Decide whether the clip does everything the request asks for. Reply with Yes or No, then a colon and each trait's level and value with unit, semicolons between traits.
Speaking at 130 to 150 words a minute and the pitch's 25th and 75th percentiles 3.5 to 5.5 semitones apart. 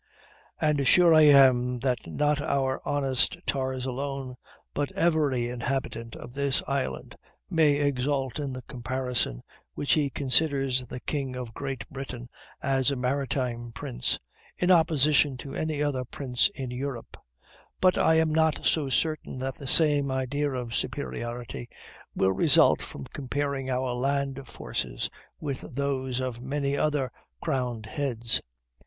No: average, 140 wpm; narrow, 2.4 semitones